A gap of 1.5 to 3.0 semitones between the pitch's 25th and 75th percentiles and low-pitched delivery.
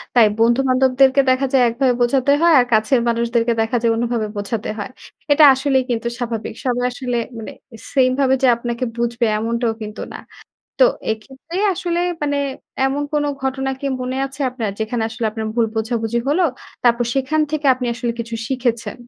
No: narrow, 2.5 semitones; high, 245 Hz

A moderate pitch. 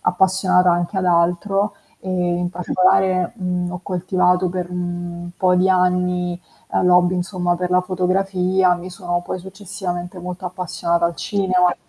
Yes: medium, 180 Hz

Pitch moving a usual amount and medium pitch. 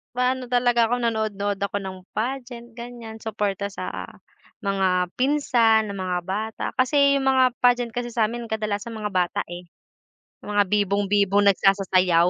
No: average, 3.5 semitones; high, 215 Hz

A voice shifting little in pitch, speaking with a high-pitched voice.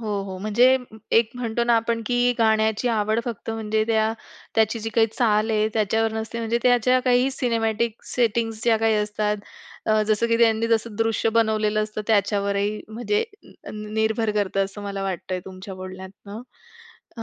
Yes: narrow, 1.6 semitones; high, 220 Hz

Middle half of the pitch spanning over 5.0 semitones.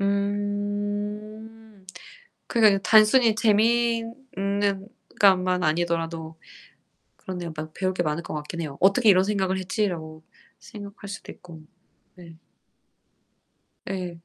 No: average, 3.3 semitones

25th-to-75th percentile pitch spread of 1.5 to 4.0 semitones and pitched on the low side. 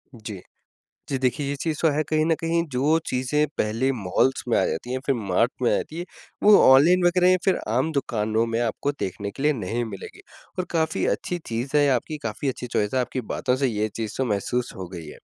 No: wide, 5.4 semitones; low, 130 Hz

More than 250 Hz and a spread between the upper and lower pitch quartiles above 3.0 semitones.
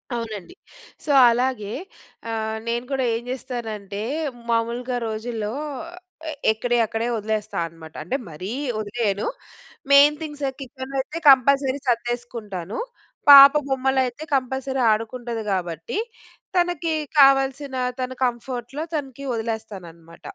No: high, 240 Hz; average, 3.6 semitones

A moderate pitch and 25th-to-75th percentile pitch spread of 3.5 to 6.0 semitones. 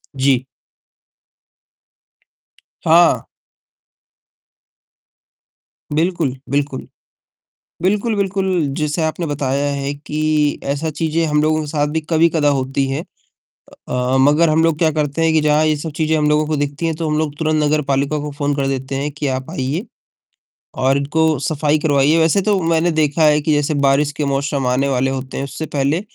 No: medium, 150 Hz; narrow, 2.4 semitones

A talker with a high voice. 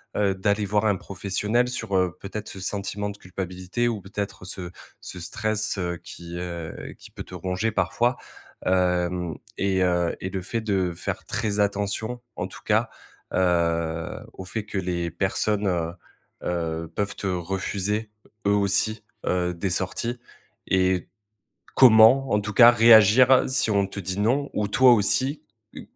No: low, 100 Hz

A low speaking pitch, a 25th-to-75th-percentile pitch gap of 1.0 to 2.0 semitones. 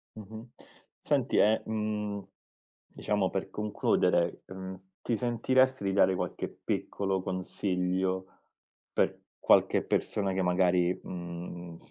No: very low, 95 Hz; narrow, 2.5 semitones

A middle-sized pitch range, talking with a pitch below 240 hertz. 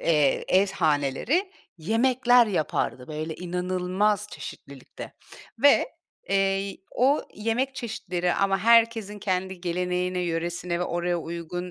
Yes: average, 4.0 semitones; medium, 185 Hz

